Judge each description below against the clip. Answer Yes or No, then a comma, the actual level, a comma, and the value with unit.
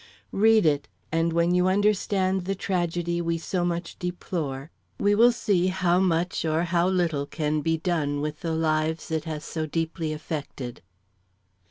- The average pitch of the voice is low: No, medium, 170 Hz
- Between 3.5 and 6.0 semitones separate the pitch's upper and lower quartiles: No, average, 2.7 semitones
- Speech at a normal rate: Yes, average, 160 wpm